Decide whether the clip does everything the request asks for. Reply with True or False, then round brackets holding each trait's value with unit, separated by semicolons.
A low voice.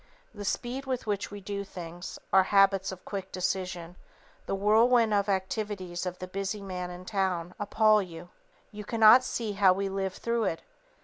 False (195 Hz)